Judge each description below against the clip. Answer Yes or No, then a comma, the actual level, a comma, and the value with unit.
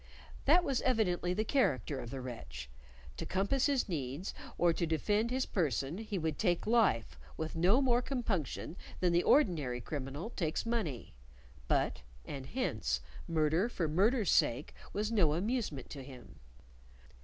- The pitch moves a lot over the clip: Yes, wide, 8.3 semitones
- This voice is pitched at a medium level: Yes, medium, 175 Hz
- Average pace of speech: Yes, average, 150 wpm